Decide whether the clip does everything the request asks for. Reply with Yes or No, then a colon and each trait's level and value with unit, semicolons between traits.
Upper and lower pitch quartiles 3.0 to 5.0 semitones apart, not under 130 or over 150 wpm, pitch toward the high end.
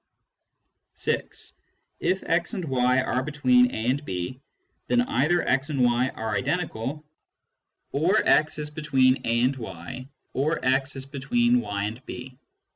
No: average, 3.6 semitones; average, 145 wpm; low, 135 Hz